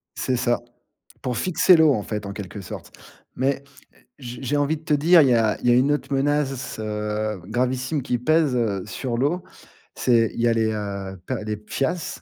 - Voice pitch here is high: No, low, 125 Hz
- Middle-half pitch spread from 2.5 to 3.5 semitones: No, average, 4.9 semitones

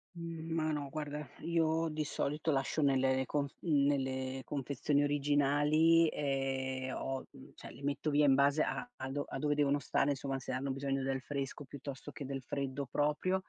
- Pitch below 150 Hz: Yes, medium, 140 Hz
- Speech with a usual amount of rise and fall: No, narrow, 1.9 semitones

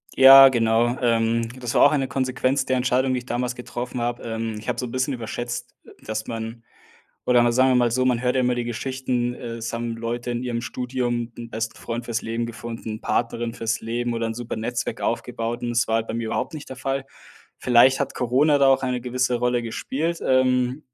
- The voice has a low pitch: Yes, low, 120 Hz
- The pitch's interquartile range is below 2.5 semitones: Yes, narrow, 1.7 semitones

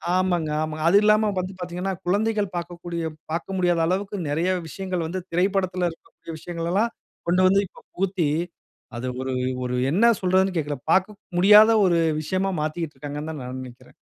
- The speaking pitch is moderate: Yes, medium, 180 Hz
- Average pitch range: Yes, average, 3.0 semitones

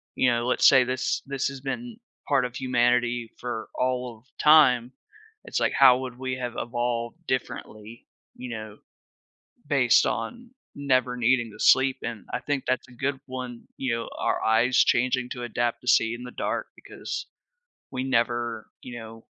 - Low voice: Yes, low, 125 Hz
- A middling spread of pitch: No, narrow, 1.6 semitones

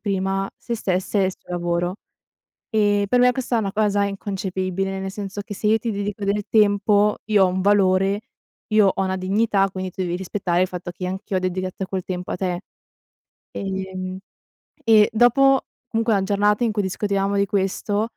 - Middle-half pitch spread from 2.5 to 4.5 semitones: No, narrow, 1.9 semitones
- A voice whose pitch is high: Yes, high, 195 Hz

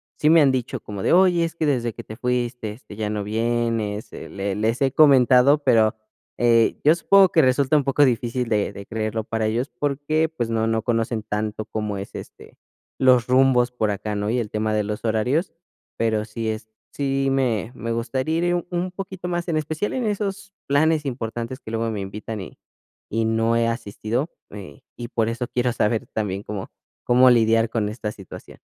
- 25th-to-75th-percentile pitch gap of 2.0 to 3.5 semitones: No, average, 4.0 semitones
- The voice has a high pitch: No, low, 115 Hz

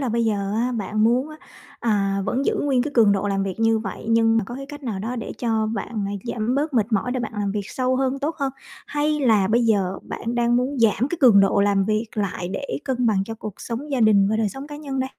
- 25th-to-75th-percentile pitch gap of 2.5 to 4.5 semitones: Yes, average, 3.9 semitones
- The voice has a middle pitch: No, high, 230 Hz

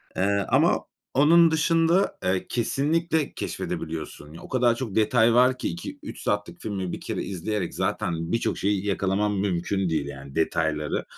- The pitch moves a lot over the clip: Yes, wide, 6.8 semitones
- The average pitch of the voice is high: No, low, 100 Hz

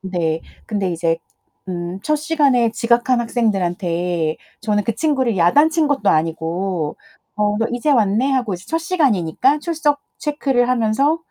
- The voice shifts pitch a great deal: Yes, wide, 7.9 semitones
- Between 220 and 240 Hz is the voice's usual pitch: Yes, high, 225 Hz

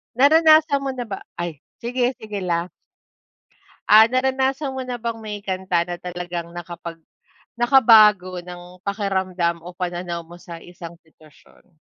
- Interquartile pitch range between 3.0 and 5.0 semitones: No, wide, 5.6 semitones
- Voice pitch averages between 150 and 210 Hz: Yes, high, 190 Hz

